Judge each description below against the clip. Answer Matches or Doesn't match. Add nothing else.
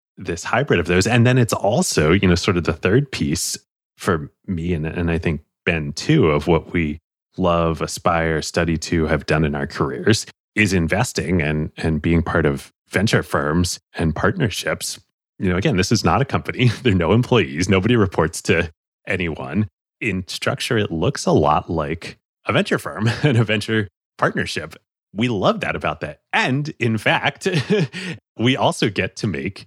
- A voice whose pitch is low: Matches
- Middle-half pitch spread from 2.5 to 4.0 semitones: Doesn't match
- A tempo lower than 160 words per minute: Doesn't match